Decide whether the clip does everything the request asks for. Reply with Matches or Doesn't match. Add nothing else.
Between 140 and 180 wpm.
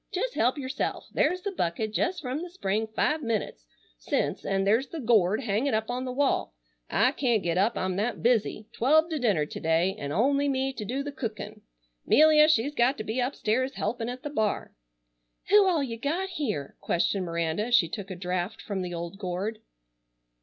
Doesn't match